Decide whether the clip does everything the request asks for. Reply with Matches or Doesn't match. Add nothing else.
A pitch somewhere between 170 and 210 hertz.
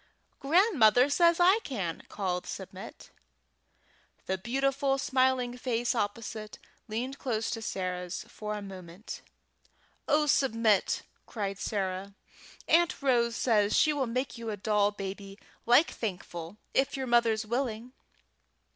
Doesn't match